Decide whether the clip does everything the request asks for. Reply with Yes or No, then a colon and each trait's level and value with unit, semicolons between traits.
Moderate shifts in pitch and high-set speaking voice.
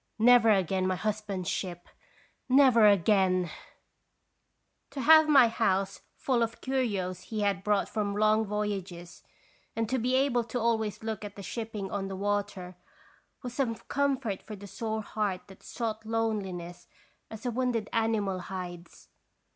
Yes: average, 3.1 semitones; high, 210 Hz